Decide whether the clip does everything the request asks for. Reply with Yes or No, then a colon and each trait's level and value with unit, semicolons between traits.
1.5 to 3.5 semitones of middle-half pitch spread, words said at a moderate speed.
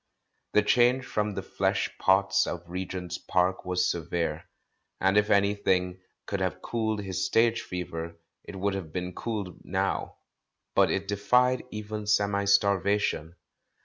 Yes: narrow, 2.4 semitones; average, 145 wpm